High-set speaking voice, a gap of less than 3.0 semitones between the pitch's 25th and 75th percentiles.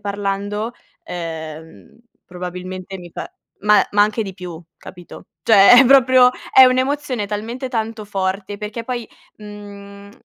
No: high, 205 Hz; average, 3.5 semitones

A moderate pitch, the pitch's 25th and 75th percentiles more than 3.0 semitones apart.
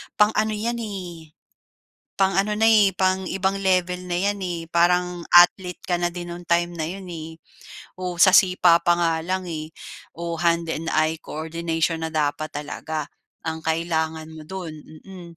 No: medium, 175 Hz; narrow, 2.6 semitones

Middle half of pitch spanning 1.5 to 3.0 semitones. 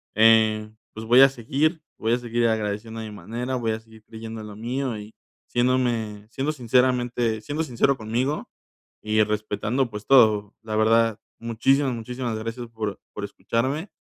Yes: narrow, 2.4 semitones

